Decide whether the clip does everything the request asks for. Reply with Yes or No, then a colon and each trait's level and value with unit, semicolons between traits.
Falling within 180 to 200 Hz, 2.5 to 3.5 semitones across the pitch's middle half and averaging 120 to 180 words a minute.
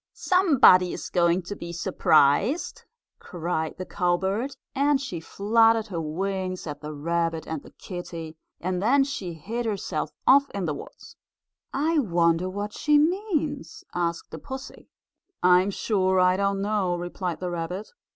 No: medium, 185 Hz; average, 4.9 semitones; average, 150 wpm